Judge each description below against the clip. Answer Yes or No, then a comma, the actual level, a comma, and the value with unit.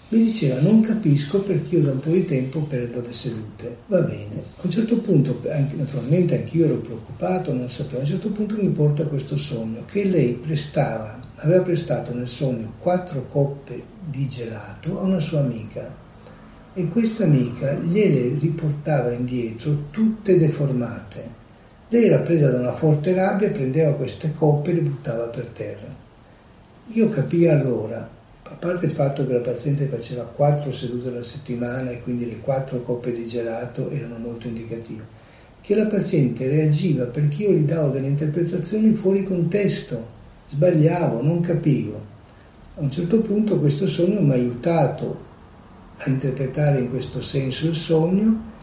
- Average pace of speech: Yes, average, 160 wpm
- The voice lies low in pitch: No, medium, 145 Hz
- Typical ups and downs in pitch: No, wide, 5.9 semitones